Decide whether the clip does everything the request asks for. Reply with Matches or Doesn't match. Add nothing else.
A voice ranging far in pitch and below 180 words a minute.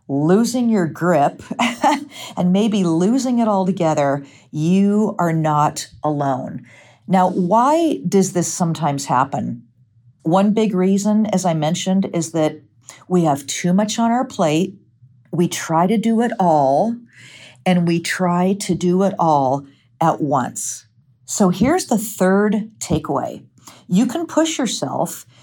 Matches